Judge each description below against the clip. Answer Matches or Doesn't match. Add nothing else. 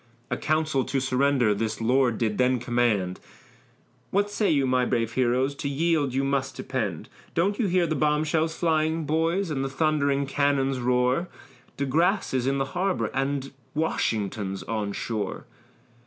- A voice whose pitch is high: Doesn't match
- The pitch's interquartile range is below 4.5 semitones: Matches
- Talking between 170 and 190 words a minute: Doesn't match